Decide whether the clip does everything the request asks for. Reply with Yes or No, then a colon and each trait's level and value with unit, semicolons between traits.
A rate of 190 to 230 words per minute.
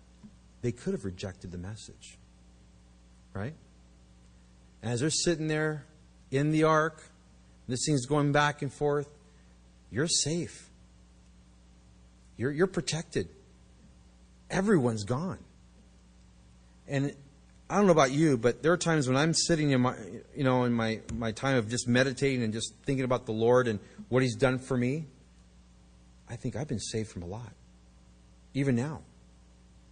No: average, 145 wpm